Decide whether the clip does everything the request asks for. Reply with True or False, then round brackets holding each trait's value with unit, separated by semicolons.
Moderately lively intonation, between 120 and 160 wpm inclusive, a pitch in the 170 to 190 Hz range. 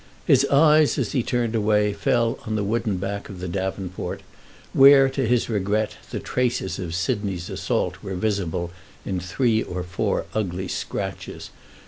False (4.1 semitones; 155 wpm; 105 Hz)